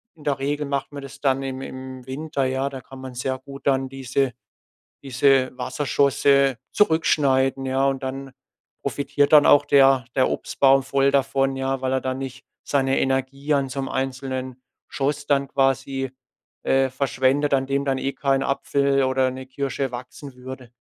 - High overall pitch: No, low, 135 Hz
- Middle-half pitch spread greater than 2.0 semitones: No, narrow, 0.9 semitones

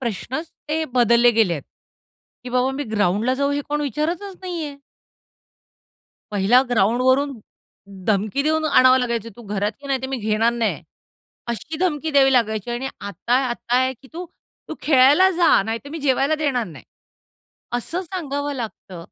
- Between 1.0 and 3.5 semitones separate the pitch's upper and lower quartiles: No, average, 4.2 semitones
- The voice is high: Yes, very high, 260 Hz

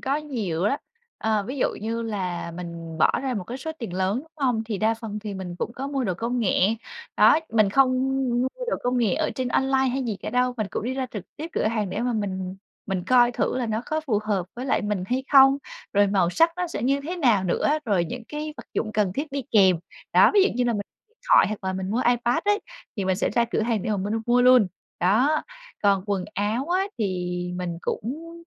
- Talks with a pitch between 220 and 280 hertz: Yes, high, 225 Hz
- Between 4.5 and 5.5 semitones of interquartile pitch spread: Yes, average, 5.1 semitones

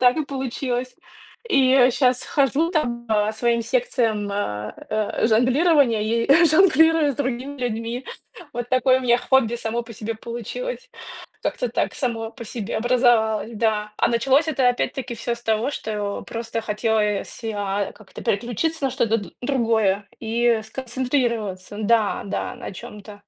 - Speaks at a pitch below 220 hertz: No, high, 235 Hz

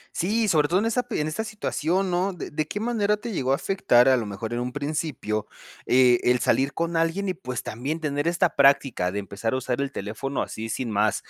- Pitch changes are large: Yes, wide, 6.8 semitones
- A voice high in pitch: No, medium, 145 Hz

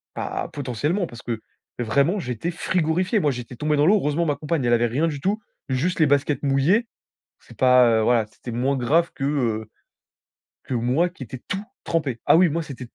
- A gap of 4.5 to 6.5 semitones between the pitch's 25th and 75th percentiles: Yes, average, 5.1 semitones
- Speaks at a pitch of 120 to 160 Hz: Yes, medium, 140 Hz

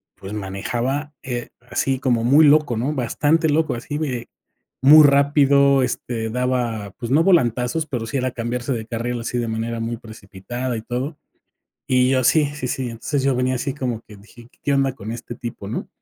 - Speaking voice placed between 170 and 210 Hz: No, low, 125 Hz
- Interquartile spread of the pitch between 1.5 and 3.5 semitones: Yes, average, 3.2 semitones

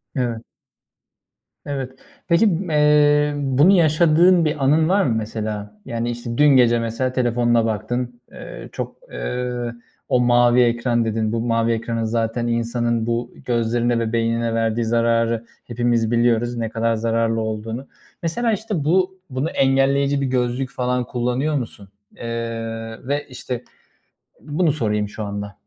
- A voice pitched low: Yes, low, 120 Hz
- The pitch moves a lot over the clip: No, average, 3.2 semitones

